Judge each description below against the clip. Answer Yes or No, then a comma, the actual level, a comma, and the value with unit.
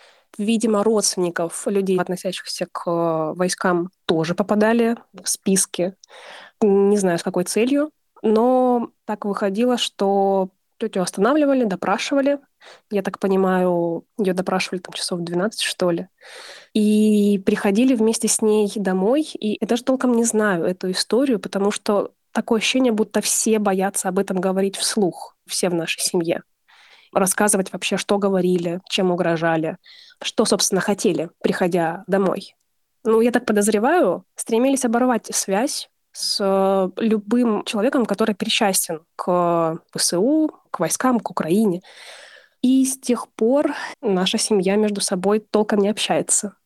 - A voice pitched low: No, high, 205 Hz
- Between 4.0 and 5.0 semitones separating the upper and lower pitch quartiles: No, average, 3.4 semitones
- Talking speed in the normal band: Yes, average, 130 wpm